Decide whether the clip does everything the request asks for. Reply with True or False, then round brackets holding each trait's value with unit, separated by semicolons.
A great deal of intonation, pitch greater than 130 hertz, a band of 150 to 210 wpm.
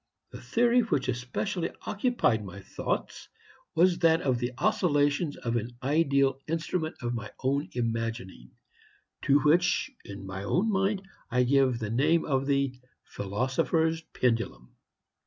False (5.8 semitones; 140 Hz; 135 wpm)